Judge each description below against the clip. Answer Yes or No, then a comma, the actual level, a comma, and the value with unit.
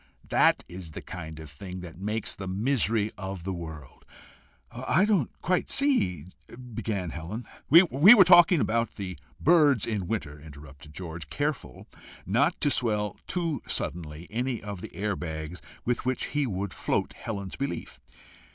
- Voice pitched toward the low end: Yes, low, 105 Hz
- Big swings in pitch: Yes, wide, 7.3 semitones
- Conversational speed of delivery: Yes, average, 155 wpm